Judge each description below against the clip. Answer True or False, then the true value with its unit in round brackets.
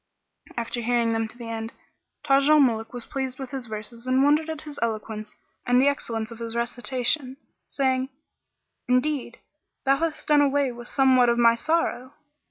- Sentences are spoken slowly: False (175 wpm)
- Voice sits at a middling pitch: False (250 Hz)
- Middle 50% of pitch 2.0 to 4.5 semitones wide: True (3.0 semitones)